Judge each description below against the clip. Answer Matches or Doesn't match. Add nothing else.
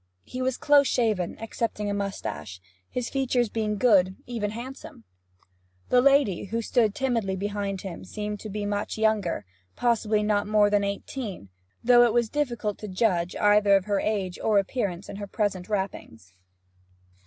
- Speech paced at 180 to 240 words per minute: Doesn't match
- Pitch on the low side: Doesn't match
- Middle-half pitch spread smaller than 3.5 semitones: Matches